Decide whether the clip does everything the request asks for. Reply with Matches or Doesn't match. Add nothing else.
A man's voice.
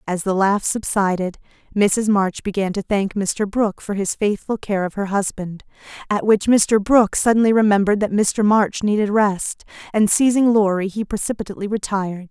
Doesn't match